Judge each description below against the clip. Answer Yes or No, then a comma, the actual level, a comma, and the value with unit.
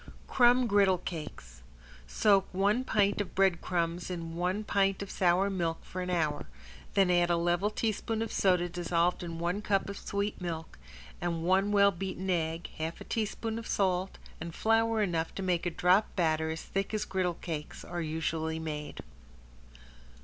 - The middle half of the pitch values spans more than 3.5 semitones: No, average, 3.0 semitones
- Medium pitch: Yes, medium, 180 Hz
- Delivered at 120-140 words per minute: No, average, 170 wpm